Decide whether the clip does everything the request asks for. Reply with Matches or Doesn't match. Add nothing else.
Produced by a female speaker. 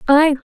Matches